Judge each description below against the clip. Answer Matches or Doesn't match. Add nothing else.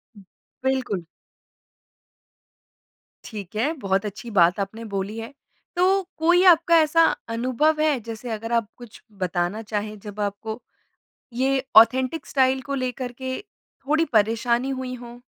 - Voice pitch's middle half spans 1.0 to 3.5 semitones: Doesn't match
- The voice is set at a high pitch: Matches